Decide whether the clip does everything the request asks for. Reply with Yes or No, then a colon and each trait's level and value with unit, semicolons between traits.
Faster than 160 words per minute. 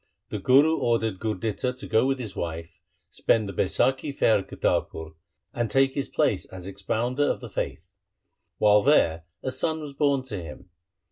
Yes: average, 175 wpm